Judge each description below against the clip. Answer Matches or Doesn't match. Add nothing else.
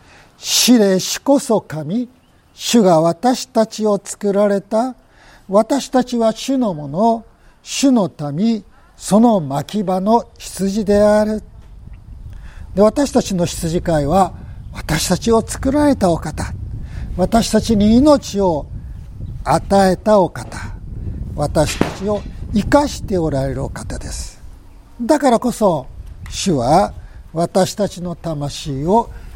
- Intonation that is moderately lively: Doesn't match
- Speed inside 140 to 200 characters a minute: Matches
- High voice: Matches